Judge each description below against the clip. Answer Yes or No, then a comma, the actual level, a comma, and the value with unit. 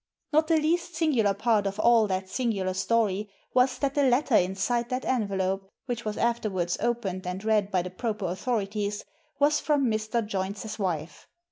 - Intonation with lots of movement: No, average, 4.4 semitones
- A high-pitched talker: Yes, high, 215 Hz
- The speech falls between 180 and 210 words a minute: No, average, 165 wpm